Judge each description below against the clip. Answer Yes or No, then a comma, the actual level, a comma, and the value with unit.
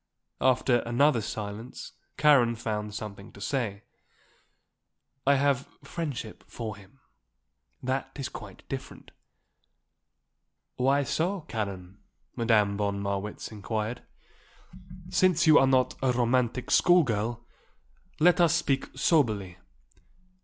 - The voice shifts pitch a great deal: No, average, 4.9 semitones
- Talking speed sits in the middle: No, slow, 105 wpm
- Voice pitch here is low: Yes, low, 120 Hz